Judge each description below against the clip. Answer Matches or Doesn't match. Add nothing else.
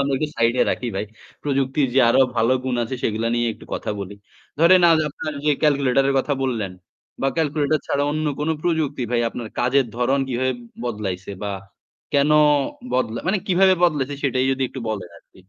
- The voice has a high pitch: Doesn't match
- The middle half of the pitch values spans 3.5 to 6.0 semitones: Matches